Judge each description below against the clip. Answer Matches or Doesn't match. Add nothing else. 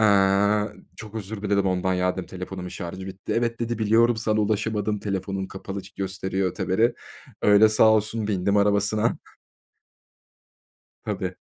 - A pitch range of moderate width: Doesn't match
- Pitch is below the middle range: Matches